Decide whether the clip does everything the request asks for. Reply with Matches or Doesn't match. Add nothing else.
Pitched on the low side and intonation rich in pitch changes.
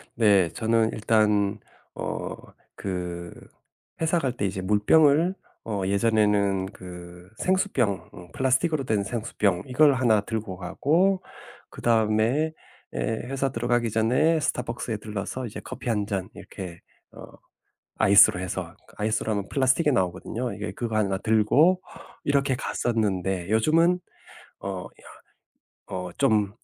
Doesn't match